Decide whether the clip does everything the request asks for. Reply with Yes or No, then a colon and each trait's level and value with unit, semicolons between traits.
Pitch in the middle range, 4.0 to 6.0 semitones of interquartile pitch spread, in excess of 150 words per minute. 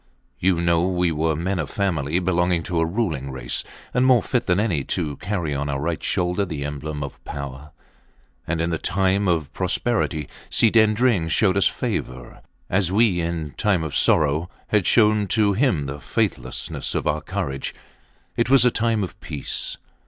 No: very low, 85 Hz; average, 5.1 semitones; average, 175 wpm